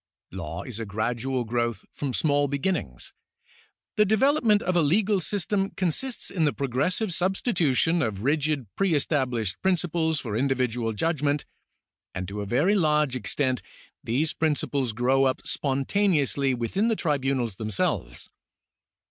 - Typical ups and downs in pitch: No, wide, 6.3 semitones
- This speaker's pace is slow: Yes, slow, 130 wpm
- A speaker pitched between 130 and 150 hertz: Yes, medium, 140 Hz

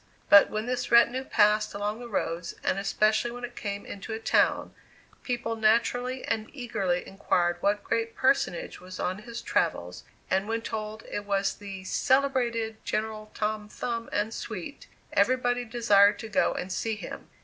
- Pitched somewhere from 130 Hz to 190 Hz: No, high, 220 Hz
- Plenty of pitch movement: No, average, 2.8 semitones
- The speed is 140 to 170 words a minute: Yes, average, 165 wpm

